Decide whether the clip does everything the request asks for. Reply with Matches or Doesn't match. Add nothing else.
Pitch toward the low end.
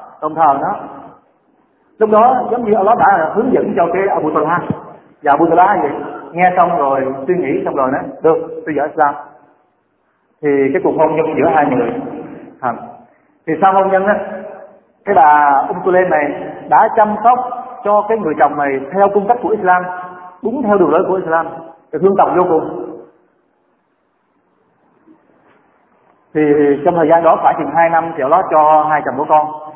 Doesn't match